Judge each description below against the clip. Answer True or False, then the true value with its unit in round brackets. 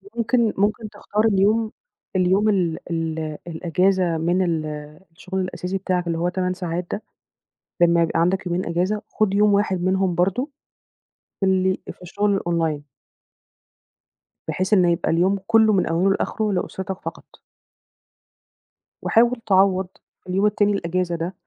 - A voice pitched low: False (185 Hz)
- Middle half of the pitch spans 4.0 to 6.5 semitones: False (2.8 semitones)